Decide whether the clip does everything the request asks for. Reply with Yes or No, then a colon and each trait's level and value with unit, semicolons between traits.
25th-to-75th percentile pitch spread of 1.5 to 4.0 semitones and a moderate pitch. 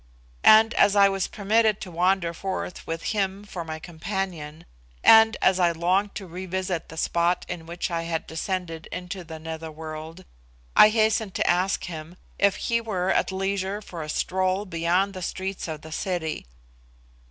Yes: average, 2.9 semitones; medium, 180 Hz